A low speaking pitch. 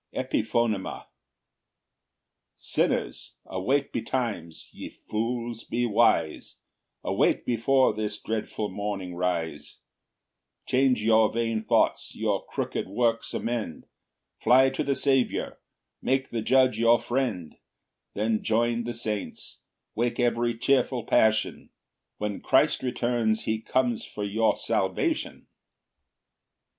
Yes: low, 115 Hz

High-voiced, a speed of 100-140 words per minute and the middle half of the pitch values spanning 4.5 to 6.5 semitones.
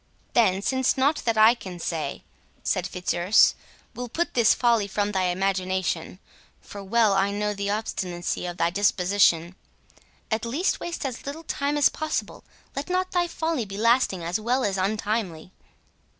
No: high, 210 Hz; average, 155 wpm; average, 4.9 semitones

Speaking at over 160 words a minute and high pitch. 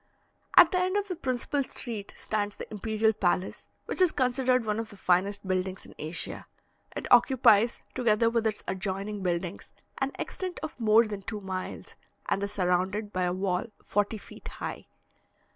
Yes: average, 170 wpm; high, 210 Hz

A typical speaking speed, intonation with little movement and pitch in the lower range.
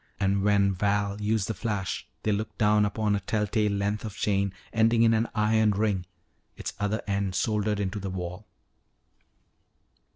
Yes: average, 160 wpm; narrow, 1.5 semitones; low, 105 Hz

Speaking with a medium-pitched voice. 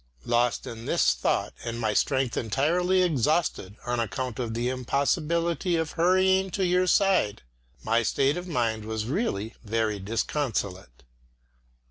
No: low, 130 Hz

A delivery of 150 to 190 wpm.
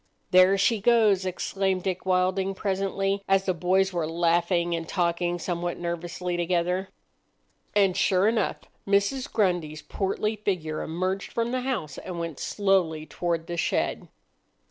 No: average, 140 wpm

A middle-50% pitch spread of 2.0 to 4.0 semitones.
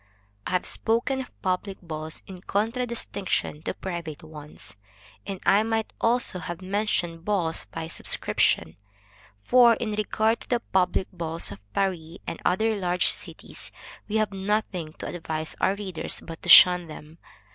No: average, 4.6 semitones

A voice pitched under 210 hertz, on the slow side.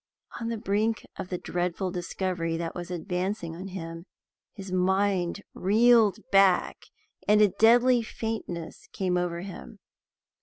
Yes: high, 190 Hz; slow, 130 wpm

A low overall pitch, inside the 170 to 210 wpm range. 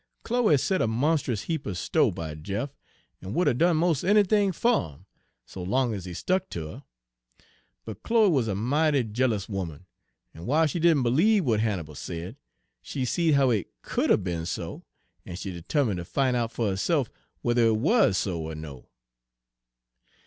Yes: low, 120 Hz; average, 180 wpm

